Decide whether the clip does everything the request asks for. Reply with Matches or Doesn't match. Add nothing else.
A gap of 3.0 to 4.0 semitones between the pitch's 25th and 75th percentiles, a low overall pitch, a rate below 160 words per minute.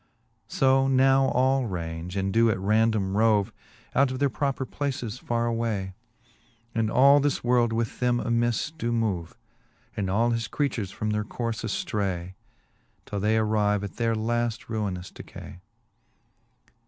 Matches